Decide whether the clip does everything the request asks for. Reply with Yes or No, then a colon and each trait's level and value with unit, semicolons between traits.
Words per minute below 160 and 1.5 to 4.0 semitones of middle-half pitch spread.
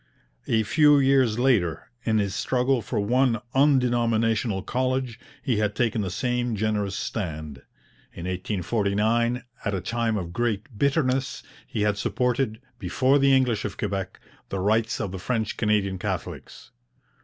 Yes: average, 145 wpm; average, 3.7 semitones